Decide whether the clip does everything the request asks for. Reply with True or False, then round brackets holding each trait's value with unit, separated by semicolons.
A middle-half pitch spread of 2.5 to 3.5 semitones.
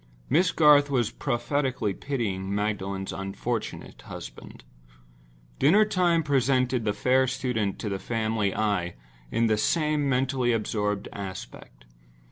False (5.1 semitones)